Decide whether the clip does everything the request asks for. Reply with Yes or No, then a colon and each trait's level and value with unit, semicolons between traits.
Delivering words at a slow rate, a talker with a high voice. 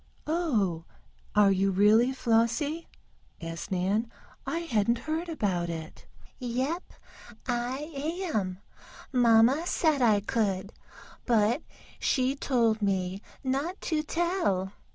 Yes: slow, 105 wpm; high, 235 Hz